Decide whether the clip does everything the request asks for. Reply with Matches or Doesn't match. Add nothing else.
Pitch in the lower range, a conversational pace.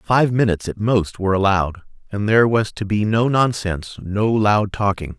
Matches